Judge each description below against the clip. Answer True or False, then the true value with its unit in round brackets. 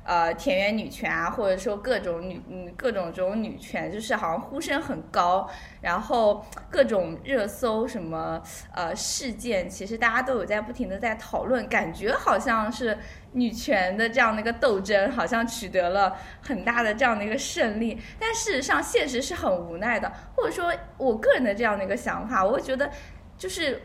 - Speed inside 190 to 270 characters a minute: False (280 characters per minute)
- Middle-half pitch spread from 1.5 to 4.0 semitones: False (5.1 semitones)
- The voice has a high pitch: True (230 Hz)